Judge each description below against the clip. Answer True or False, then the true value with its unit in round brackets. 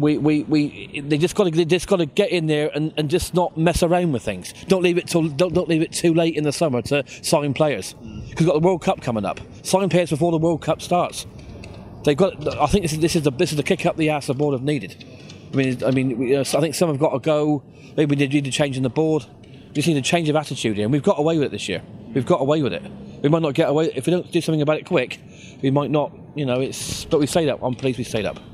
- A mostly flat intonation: False (3.7 semitones)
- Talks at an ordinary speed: False (305 wpm)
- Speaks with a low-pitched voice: False (150 Hz)